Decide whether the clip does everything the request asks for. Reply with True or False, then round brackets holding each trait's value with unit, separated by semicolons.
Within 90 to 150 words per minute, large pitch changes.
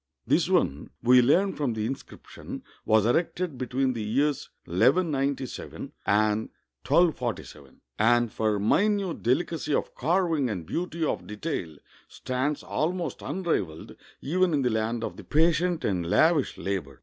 True (135 wpm; 7.3 semitones)